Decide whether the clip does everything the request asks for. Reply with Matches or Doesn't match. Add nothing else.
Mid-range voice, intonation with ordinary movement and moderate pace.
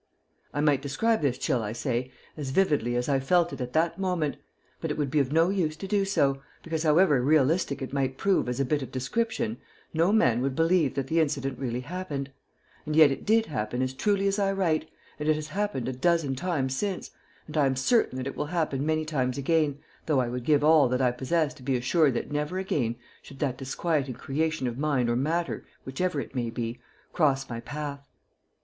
Doesn't match